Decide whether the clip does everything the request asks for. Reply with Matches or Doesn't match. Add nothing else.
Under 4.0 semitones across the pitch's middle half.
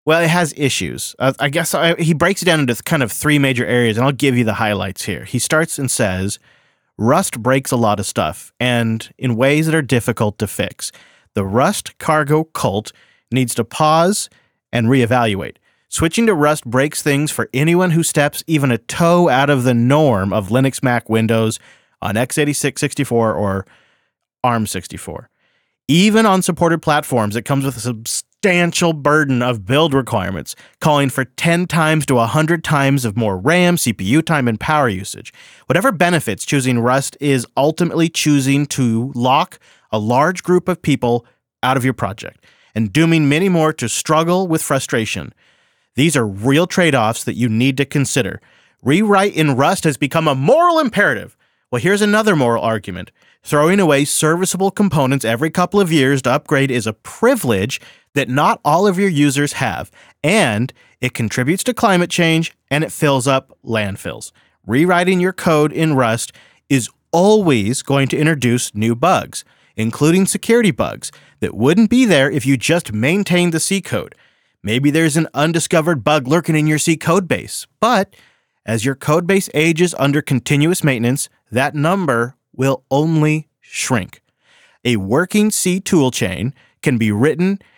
Doesn't match